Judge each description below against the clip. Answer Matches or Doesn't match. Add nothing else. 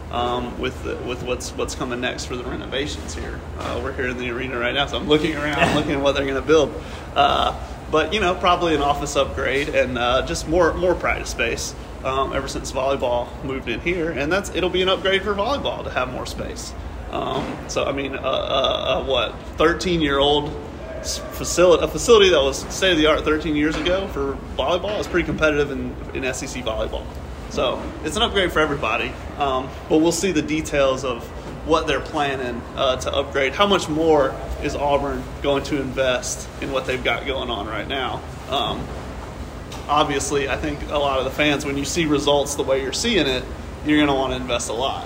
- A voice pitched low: Doesn't match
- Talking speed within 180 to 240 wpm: Matches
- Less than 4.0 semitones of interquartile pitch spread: Matches